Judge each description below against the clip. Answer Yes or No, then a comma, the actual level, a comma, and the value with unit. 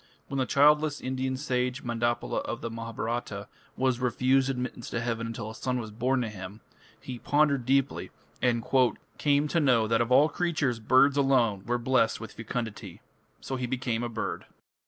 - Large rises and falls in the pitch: No, average, 2.7 semitones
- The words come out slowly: No, average, 175 wpm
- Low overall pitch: Yes, low, 125 Hz